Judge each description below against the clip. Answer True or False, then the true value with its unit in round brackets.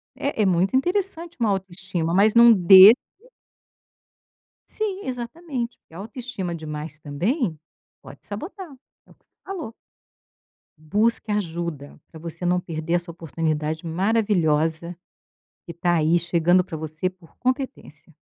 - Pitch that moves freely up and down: True (6.1 semitones)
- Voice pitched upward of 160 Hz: True (185 Hz)